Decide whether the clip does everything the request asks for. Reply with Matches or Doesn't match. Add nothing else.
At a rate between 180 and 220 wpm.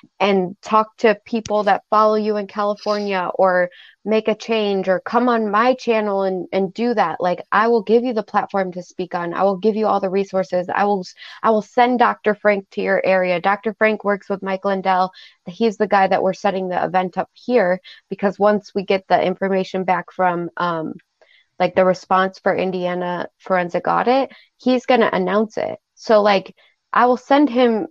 Matches